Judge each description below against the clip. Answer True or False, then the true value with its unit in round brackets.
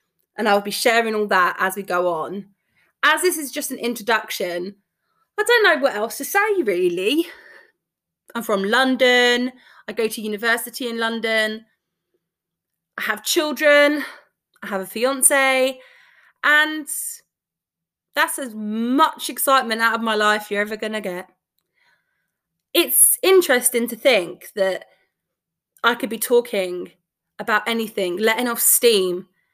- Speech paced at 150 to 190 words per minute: False (140 wpm)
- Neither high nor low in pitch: False (235 Hz)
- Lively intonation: True (6.0 semitones)